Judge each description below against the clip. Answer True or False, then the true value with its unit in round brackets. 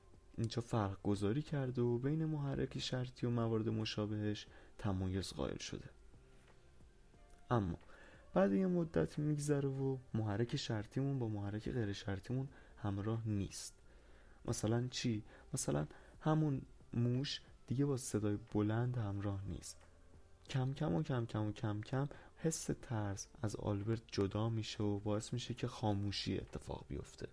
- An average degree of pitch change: True (4.0 semitones)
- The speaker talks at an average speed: True (130 wpm)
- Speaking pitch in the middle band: False (110 Hz)